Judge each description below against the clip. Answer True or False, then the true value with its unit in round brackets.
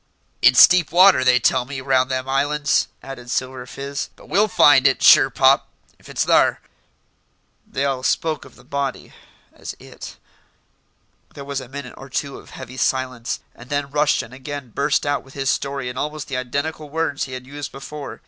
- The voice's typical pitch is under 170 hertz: True (135 Hz)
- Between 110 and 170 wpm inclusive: False (185 wpm)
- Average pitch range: False (1.9 semitones)